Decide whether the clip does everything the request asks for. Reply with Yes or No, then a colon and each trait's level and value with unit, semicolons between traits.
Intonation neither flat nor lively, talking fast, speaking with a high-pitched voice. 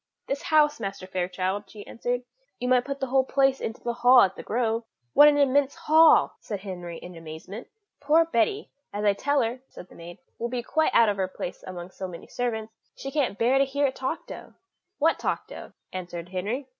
No: wide, 6.3 semitones; fast, 210 wpm; high, 235 Hz